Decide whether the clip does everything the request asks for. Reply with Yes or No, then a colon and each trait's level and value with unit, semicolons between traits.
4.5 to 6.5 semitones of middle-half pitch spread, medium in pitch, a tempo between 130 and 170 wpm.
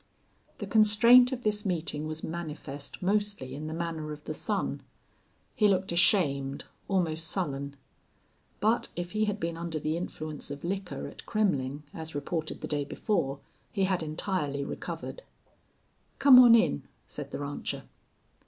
Yes: wide, 5.6 semitones; medium, 170 Hz; average, 150 wpm